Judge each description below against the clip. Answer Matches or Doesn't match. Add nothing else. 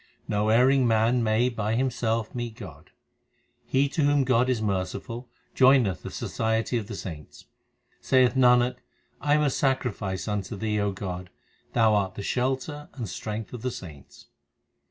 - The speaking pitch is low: Matches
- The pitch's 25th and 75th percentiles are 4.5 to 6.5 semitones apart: Doesn't match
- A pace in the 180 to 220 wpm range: Doesn't match